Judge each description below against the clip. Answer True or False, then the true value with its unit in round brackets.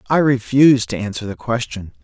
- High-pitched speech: False (115 Hz)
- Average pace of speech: True (175 wpm)